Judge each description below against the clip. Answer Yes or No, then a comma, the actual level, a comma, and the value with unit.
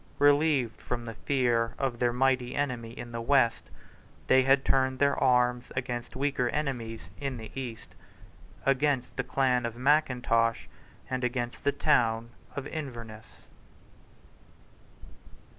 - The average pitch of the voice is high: No, low, 125 Hz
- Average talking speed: No, slow, 125 wpm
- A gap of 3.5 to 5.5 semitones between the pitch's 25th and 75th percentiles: No, narrow, 2.4 semitones